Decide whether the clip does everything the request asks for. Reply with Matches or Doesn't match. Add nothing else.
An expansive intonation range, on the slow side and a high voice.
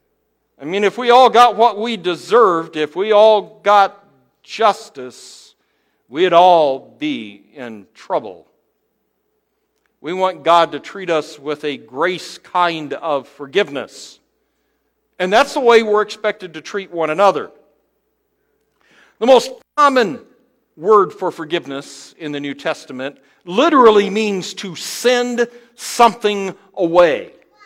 Matches